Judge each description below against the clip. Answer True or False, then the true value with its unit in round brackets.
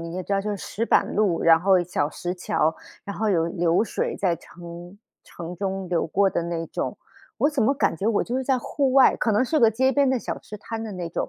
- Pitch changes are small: False (4.9 semitones)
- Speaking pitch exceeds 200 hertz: False (195 Hz)